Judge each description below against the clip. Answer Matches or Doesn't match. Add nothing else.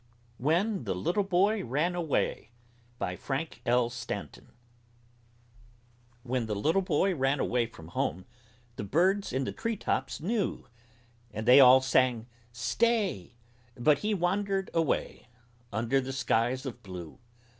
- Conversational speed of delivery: Doesn't match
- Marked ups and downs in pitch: Matches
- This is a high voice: Doesn't match